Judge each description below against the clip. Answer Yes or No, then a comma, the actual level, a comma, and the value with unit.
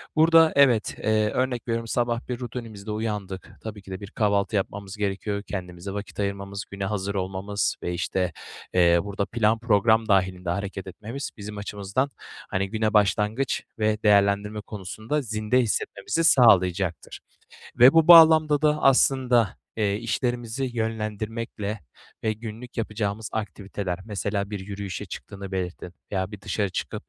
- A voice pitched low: Yes, low, 105 Hz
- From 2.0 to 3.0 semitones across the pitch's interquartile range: Yes, average, 2.7 semitones